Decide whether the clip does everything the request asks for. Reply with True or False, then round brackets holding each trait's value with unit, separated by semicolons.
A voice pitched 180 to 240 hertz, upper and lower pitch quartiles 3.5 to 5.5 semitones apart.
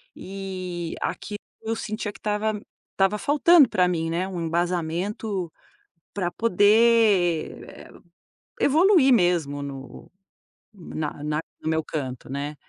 True (185 Hz; 4.8 semitones)